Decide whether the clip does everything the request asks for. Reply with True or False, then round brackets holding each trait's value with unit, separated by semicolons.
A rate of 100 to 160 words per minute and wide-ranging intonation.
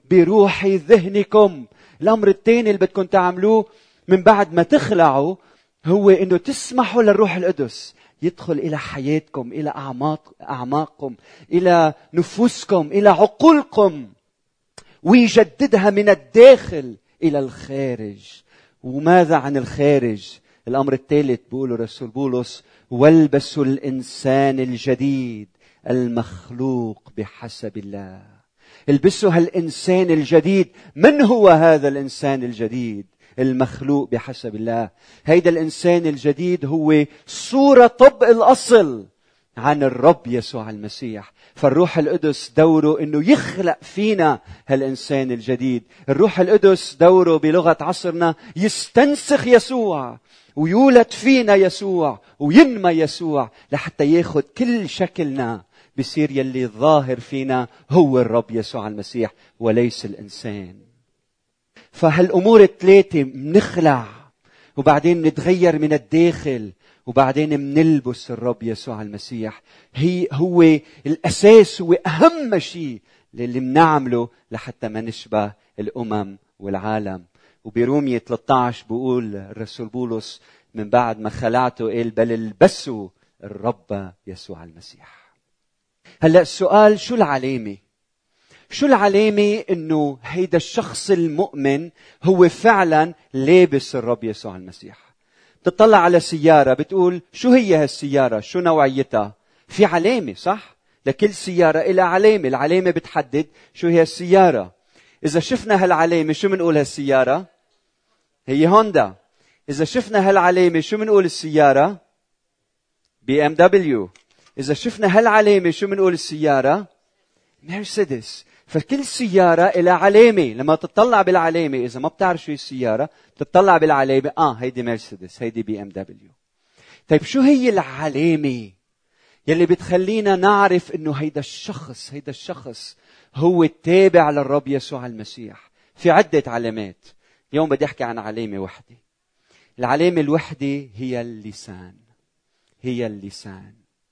True (105 wpm; 6.8 semitones)